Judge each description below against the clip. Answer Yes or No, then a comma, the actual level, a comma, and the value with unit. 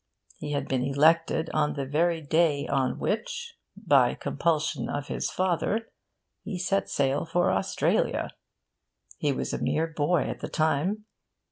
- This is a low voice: No, medium, 160 Hz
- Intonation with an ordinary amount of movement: Yes, average, 3.6 semitones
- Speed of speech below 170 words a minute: Yes, average, 145 wpm